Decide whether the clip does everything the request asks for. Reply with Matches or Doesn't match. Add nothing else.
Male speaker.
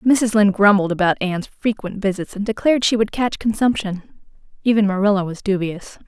Doesn't match